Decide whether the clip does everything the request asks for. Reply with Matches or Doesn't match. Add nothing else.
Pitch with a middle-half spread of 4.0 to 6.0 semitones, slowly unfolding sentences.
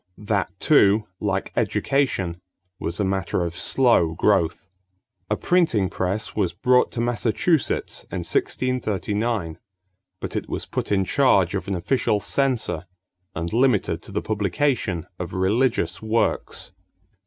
Matches